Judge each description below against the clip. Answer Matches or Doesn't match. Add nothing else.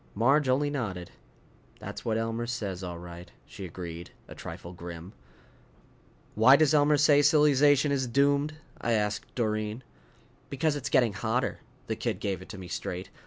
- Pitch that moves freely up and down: Matches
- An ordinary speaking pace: Matches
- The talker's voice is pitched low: Matches